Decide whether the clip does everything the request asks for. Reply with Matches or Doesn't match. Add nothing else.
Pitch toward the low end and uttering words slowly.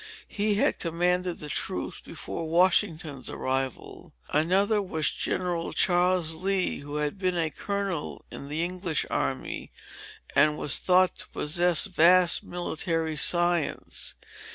Doesn't match